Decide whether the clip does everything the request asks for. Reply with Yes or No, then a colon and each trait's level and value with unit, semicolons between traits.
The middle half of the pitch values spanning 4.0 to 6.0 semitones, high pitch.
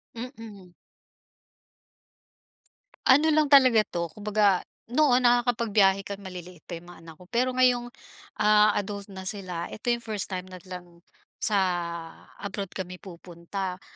Yes: average, 4.5 semitones; high, 200 Hz